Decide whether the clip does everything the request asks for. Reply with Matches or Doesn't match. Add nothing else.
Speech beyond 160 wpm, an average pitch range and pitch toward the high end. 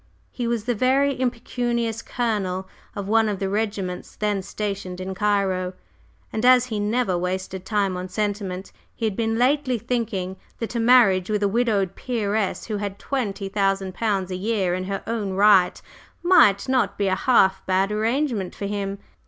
Matches